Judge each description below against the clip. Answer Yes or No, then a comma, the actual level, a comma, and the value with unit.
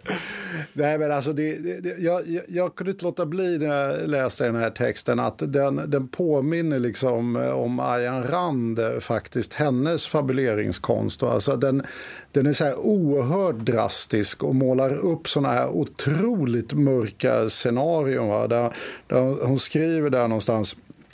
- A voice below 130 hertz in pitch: No, medium, 140 Hz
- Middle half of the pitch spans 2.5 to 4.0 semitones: No, average, 4.6 semitones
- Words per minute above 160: No, average, 150 wpm